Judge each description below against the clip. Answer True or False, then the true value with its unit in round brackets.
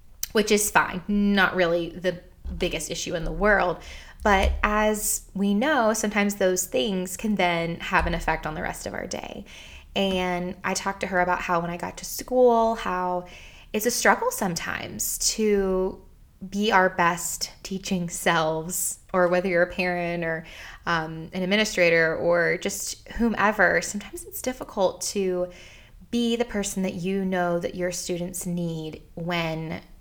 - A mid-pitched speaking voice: True (180 Hz)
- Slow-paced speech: False (160 wpm)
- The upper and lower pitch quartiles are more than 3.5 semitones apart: False (2.9 semitones)